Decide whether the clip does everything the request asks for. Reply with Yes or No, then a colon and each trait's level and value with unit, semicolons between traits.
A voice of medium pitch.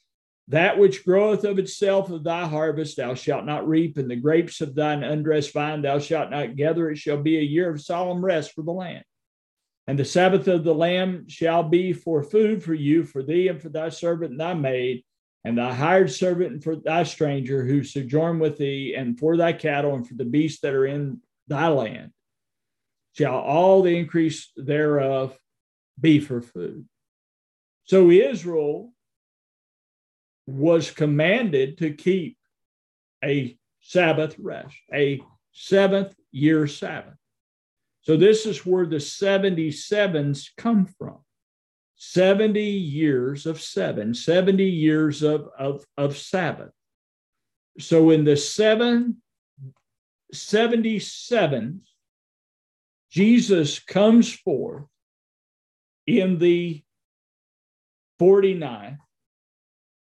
Yes: medium, 160 Hz